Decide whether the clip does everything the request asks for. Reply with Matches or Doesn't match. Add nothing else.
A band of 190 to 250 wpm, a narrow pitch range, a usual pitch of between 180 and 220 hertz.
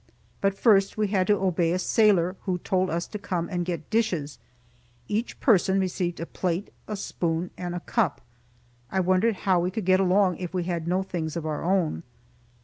Matches